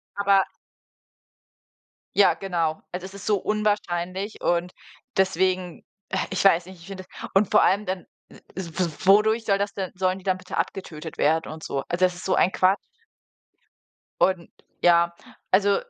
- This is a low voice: No, medium, 185 Hz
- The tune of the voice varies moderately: No, narrow, 2.1 semitones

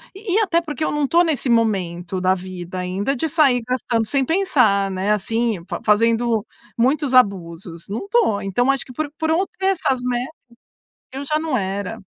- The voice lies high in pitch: Yes, high, 240 Hz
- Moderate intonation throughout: No, wide, 7.2 semitones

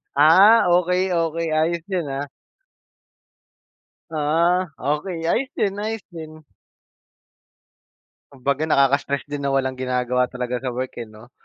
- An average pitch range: Yes, average, 4.8 semitones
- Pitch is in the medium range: Yes, medium, 150 Hz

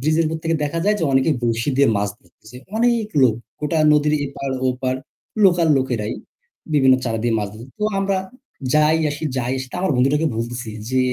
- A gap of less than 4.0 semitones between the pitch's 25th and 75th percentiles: No, average, 4.8 semitones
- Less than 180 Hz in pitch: Yes, low, 135 Hz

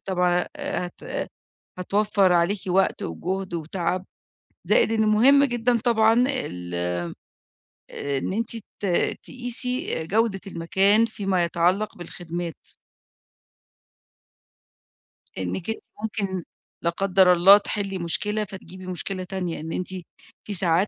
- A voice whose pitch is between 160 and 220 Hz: Yes, high, 190 Hz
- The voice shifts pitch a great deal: No, average, 3.6 semitones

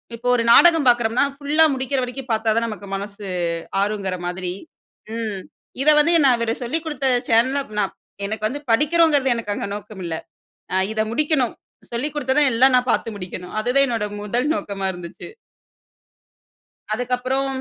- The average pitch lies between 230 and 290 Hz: Yes, high, 240 Hz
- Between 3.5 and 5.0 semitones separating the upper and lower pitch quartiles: Yes, average, 4.5 semitones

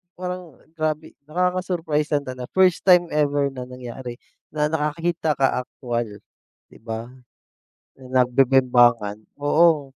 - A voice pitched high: No, medium, 145 Hz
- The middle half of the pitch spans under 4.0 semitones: No, average, 4.4 semitones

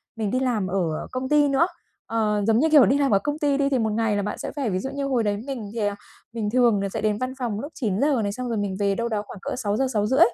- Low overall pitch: No, high, 230 Hz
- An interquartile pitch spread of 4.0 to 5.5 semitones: Yes, average, 4.6 semitones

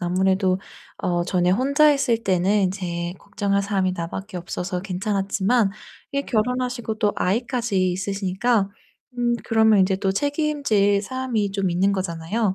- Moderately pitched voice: No, high, 200 Hz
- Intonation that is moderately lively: Yes, average, 3.8 semitones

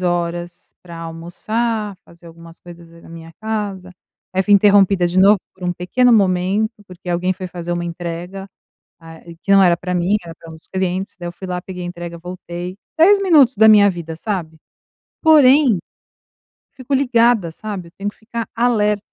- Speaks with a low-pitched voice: No, medium, 185 Hz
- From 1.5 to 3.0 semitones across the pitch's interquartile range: No, average, 3.4 semitones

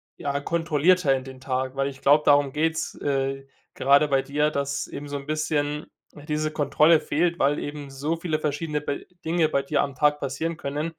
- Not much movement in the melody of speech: Yes, narrow, 1.8 semitones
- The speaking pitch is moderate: Yes, medium, 145 Hz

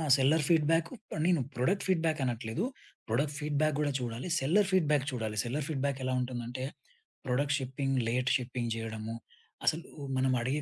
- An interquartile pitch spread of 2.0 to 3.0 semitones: No, average, 3.7 semitones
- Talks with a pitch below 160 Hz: Yes, low, 135 Hz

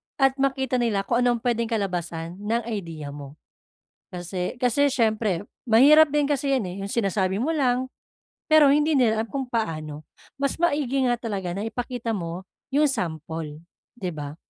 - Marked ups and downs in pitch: Yes, wide, 6.7 semitones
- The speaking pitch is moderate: No, high, 230 Hz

